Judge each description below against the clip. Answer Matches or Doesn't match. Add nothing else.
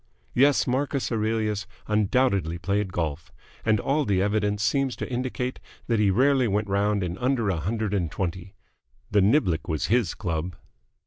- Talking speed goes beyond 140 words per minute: Matches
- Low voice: Matches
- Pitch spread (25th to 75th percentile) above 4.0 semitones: Matches